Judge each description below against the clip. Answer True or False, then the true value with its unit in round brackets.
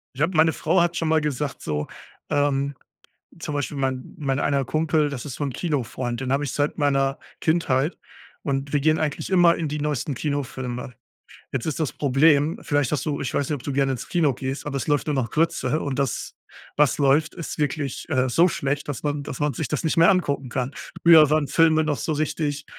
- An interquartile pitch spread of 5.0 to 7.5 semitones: False (2.4 semitones)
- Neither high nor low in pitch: True (145 Hz)